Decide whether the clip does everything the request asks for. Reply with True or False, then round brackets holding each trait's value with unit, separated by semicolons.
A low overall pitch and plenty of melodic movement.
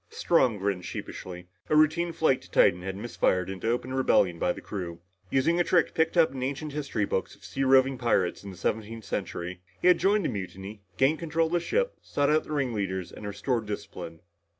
True (120 Hz; 8.1 semitones)